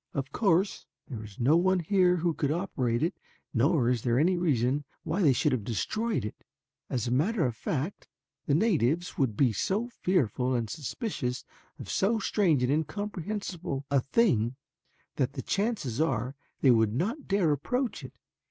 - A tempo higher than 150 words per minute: Yes, average, 170 wpm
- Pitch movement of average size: No, wide, 7.1 semitones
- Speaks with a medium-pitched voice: Yes, medium, 150 Hz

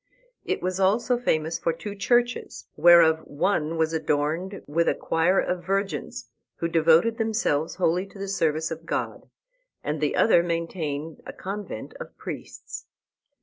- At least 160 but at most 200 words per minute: No, average, 150 wpm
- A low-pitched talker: No, medium, 170 Hz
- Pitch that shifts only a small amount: No, average, 3.5 semitones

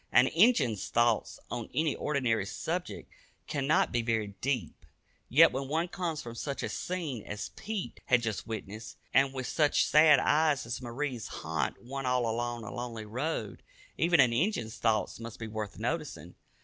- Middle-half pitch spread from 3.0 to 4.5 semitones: No, average, 5.0 semitones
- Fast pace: No, average, 165 wpm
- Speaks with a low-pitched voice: Yes, low, 125 Hz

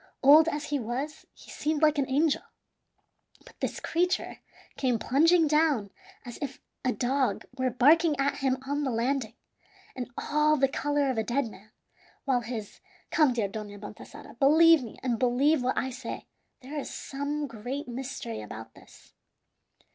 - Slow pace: No, average, 160 wpm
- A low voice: No, very high, 270 Hz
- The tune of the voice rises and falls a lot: No, average, 3.6 semitones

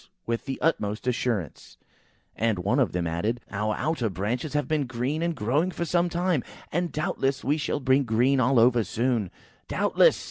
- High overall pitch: No, low, 125 Hz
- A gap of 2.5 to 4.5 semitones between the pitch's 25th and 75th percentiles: No, wide, 5.4 semitones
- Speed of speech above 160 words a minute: Yes, average, 175 wpm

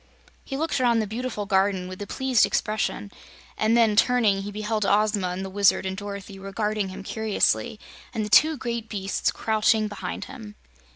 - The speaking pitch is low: No, high, 210 Hz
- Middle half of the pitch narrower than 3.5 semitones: Yes, narrow, 2.5 semitones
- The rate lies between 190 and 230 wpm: No, average, 175 wpm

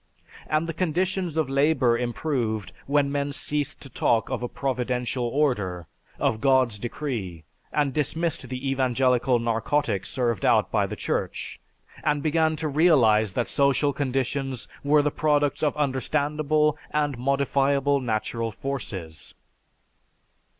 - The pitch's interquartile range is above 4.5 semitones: No, average, 3.6 semitones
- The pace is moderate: No, slow, 130 wpm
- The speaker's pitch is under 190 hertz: Yes, low, 135 Hz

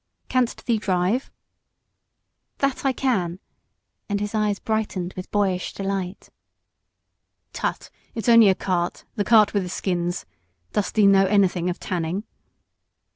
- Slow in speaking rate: Yes, slow, 130 wpm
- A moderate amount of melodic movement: Yes, average, 3.0 semitones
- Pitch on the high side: Yes, high, 200 Hz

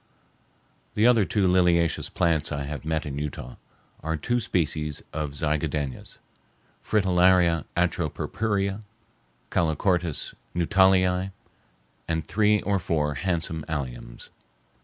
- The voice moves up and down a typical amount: Yes, average, 3.7 semitones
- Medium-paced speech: No, slow, 95 wpm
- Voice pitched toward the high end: No, very low, 85 Hz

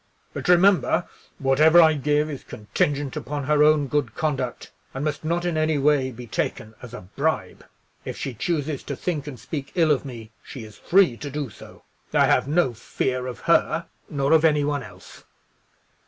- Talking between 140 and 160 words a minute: No, average, 185 wpm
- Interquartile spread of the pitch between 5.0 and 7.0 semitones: No, average, 3.2 semitones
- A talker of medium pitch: Yes, medium, 145 Hz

